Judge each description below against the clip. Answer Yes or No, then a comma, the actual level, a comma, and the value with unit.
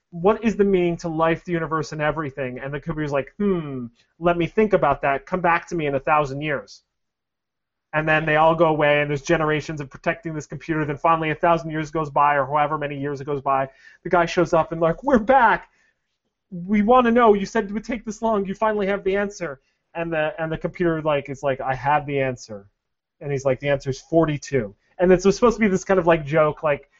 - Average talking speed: No, fast, 245 wpm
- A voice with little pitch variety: No, average, 3.6 semitones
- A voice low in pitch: No, medium, 160 Hz